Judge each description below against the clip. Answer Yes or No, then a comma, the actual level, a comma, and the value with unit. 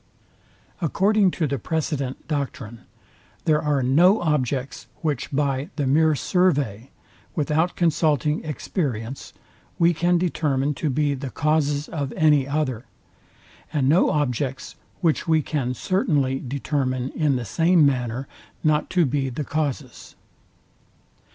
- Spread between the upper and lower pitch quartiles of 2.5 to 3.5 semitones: Yes, average, 3.1 semitones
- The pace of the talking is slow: Yes, slow, 125 wpm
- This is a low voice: No, medium, 145 Hz